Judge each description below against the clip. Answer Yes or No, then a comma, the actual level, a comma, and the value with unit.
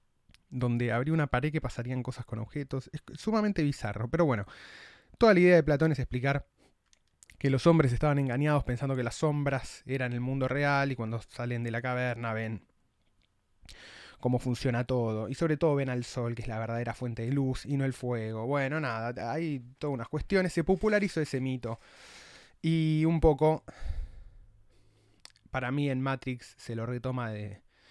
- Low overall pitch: Yes, low, 130 Hz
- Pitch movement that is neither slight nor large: Yes, average, 4.0 semitones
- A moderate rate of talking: Yes, average, 175 wpm